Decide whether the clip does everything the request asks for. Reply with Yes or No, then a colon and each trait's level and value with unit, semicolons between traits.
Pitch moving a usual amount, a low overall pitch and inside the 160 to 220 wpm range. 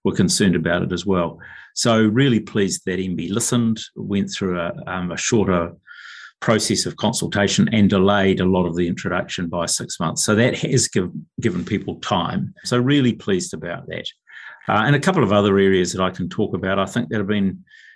Yes: average, 3.3 semitones; low, 100 Hz; average, 200 wpm